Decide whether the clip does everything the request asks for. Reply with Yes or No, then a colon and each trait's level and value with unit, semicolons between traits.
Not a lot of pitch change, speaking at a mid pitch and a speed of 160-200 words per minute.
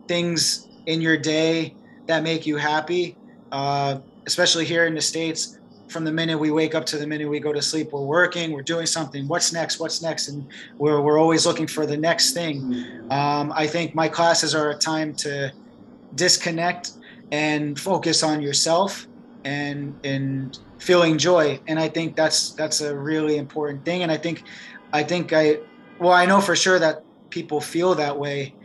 Yes: narrow, 2.1 semitones; medium, 155 Hz; average, 185 wpm